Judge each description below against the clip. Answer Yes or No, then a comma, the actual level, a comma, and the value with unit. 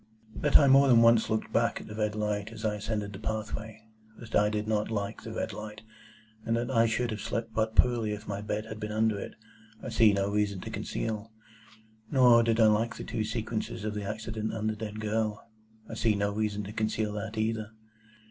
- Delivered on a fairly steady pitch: Yes, narrow, 1.2 semitones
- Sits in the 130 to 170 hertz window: No, low, 110 Hz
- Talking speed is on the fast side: Yes, fast, 220 wpm